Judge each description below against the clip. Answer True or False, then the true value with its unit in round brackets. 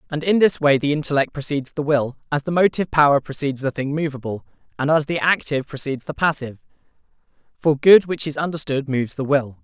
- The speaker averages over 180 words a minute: True (200 wpm)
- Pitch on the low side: False (145 Hz)